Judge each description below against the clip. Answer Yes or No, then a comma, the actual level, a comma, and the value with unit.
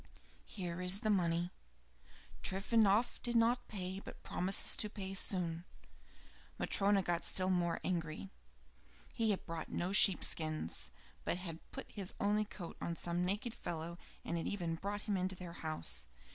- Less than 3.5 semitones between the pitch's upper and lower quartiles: Yes, average, 3.1 semitones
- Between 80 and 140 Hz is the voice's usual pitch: No, medium, 185 Hz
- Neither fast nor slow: Yes, average, 155 wpm